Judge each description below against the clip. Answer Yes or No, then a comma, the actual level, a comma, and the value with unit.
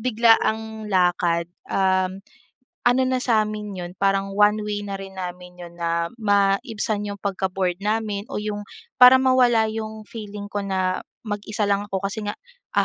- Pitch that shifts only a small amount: Yes, narrow, 2.2 semitones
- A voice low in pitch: No, high, 205 Hz